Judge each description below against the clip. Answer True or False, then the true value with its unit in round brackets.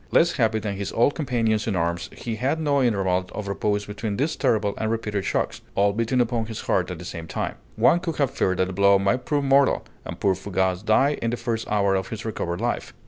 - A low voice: True (110 Hz)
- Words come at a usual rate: False (235 wpm)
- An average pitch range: True (3.8 semitones)